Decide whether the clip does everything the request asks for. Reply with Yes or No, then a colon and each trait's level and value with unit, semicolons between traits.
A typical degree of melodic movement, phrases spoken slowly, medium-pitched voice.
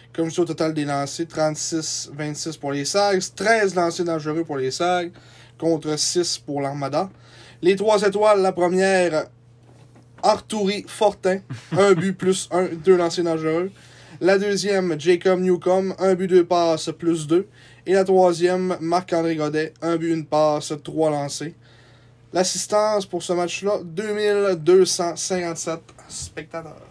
Yes: average, 3.5 semitones; slow, 140 wpm; medium, 170 Hz